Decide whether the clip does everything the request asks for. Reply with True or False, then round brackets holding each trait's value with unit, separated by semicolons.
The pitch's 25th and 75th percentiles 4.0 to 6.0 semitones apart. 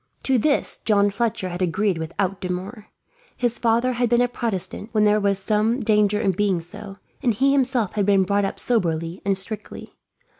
False (3.5 semitones)